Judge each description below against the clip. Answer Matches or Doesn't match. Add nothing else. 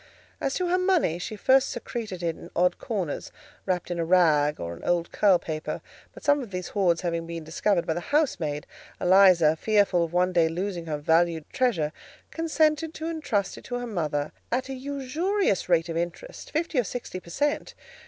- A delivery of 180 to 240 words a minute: Matches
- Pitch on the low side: Doesn't match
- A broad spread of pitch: Matches